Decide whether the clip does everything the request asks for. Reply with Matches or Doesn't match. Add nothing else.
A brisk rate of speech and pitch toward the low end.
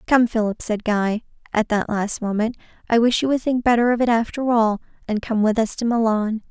Doesn't match